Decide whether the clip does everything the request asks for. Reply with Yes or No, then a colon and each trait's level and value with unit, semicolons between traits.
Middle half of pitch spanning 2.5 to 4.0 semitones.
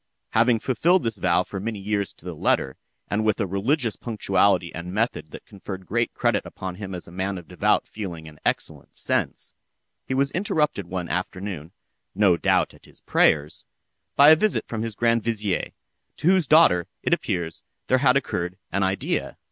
No: average, 4.6 semitones